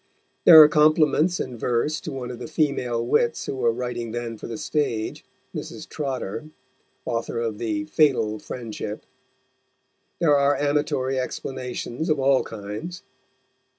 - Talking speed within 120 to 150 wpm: Yes, average, 140 wpm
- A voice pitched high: No, low, 130 Hz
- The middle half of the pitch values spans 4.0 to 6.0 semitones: Yes, average, 4.4 semitones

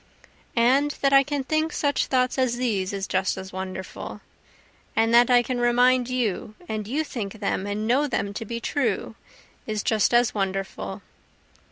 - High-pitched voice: Yes, high, 235 Hz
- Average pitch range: Yes, average, 4.0 semitones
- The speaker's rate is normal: Yes, average, 170 wpm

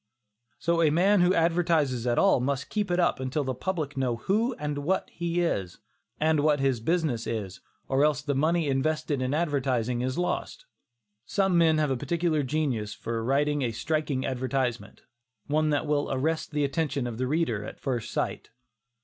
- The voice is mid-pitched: Yes, medium, 145 Hz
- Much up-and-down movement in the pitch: No, average, 4.2 semitones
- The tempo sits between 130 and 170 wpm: No, average, 180 wpm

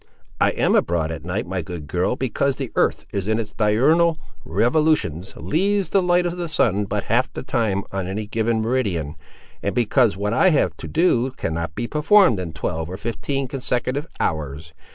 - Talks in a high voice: No, low, 110 Hz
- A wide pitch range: Yes, wide, 7.3 semitones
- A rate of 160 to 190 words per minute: Yes, average, 180 wpm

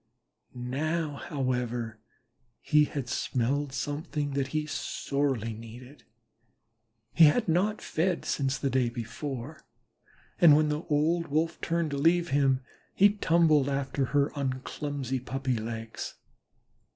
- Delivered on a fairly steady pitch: No, average, 3.3 semitones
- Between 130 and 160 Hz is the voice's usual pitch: Yes, medium, 140 Hz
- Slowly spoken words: Yes, slow, 125 wpm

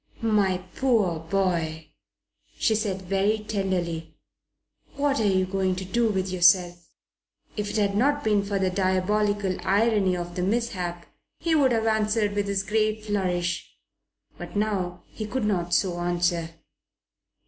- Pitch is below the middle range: No, high, 195 Hz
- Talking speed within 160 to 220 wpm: No, average, 145 wpm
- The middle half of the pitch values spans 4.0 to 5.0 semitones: No, average, 3.1 semitones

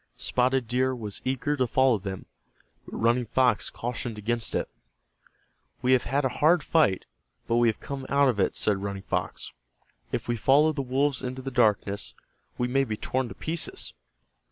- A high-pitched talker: No, low, 125 Hz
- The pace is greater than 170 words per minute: Yes, average, 180 wpm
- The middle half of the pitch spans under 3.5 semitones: Yes, average, 2.9 semitones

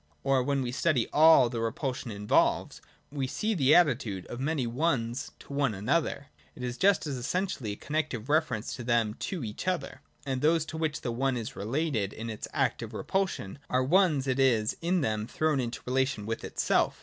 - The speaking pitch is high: No, low, 130 Hz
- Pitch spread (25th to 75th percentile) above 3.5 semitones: Yes, average, 5.0 semitones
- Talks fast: Yes, fast, 210 wpm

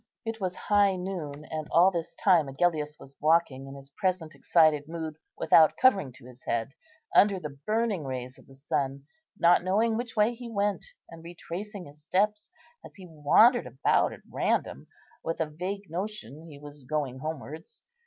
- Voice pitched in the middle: Yes, medium, 165 Hz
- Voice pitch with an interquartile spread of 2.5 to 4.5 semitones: No, average, 5.2 semitones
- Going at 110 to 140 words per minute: No, average, 175 wpm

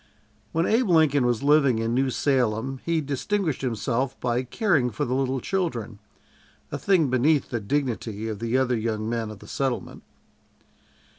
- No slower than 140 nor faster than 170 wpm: Yes, average, 160 wpm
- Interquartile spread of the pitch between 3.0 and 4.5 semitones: Yes, average, 4.0 semitones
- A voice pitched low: Yes, low, 130 Hz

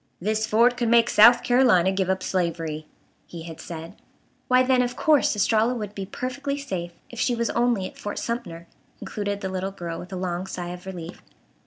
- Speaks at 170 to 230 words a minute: Yes, average, 195 wpm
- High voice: Yes, high, 200 Hz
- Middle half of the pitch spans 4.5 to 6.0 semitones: Yes, average, 5.1 semitones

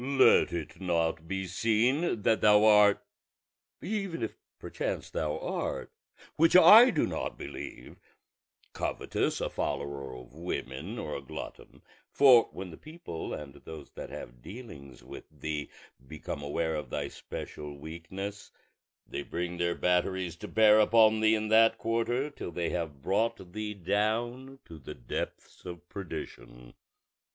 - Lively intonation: Yes, wide, 6.1 semitones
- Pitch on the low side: Yes, very low, 95 Hz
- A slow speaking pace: No, average, 145 wpm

